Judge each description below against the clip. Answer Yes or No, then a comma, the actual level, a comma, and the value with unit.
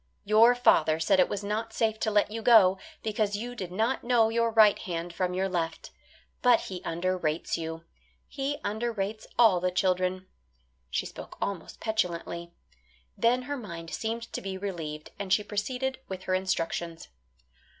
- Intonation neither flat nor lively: Yes, average, 4.0 semitones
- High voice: Yes, high, 200 Hz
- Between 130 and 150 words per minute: No, average, 170 wpm